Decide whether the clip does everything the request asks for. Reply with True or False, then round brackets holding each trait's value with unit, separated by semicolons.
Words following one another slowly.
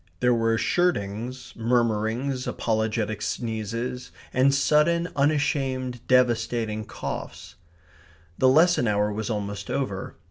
True (100 wpm)